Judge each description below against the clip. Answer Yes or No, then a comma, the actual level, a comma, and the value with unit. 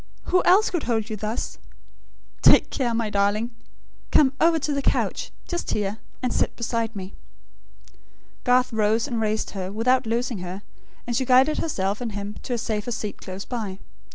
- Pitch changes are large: No, average, 3.4 semitones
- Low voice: No, high, 230 Hz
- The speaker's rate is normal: Yes, average, 175 wpm